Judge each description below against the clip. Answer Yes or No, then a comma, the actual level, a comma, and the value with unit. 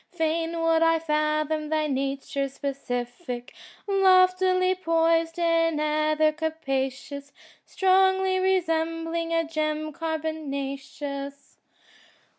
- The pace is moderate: No, slow, 80 wpm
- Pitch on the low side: No, very high, 315 Hz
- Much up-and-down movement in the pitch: No, average, 2.7 semitones